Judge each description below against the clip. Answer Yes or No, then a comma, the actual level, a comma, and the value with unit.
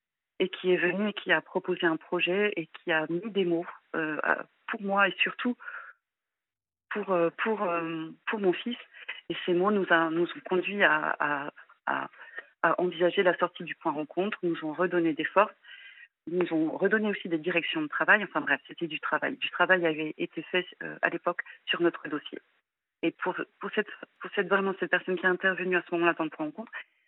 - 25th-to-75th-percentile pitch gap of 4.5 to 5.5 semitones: No, narrow, 2.6 semitones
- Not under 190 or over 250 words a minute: Yes, average, 205 wpm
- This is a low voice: No, medium, 180 Hz